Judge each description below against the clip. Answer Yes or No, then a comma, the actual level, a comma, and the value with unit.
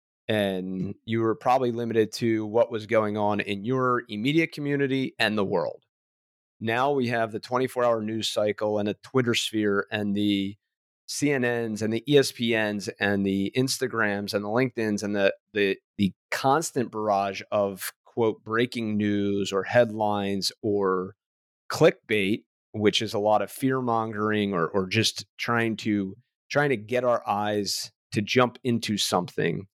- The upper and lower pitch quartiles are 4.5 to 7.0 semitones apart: No, average, 2.9 semitones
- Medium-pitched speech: No, low, 110 Hz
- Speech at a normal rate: Yes, average, 150 wpm